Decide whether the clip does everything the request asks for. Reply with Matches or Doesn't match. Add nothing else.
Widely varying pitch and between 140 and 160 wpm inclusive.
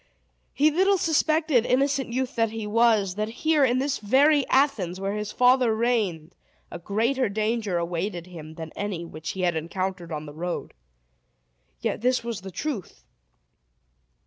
Matches